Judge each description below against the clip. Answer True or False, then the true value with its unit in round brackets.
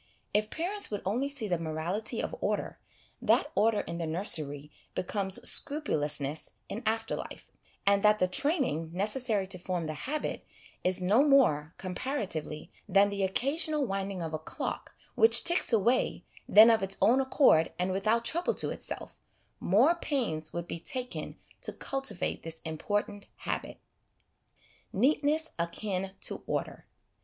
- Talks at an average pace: True (145 wpm)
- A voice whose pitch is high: True (205 Hz)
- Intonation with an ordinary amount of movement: False (7.0 semitones)